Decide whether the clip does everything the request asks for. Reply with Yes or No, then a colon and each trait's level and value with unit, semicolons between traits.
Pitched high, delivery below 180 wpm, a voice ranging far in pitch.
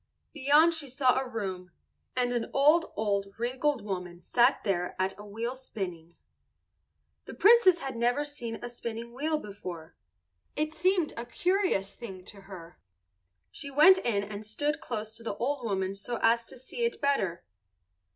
Yes: high, 235 Hz; average, 160 wpm; wide, 6.4 semitones